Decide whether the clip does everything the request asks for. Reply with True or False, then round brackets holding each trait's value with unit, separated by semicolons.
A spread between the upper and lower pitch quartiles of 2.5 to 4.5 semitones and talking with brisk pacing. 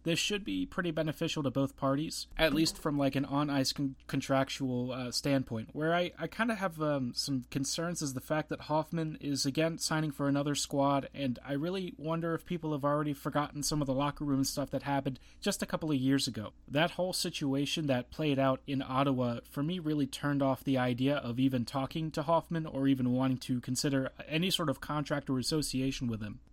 True (2.8 semitones; 215 wpm)